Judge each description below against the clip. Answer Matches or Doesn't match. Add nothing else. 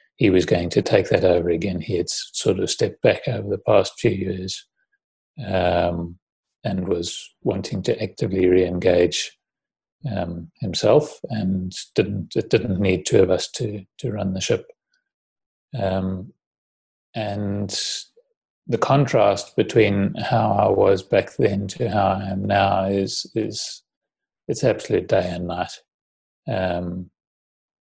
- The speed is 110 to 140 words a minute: Matches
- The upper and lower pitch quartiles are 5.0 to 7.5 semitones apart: Matches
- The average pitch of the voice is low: Matches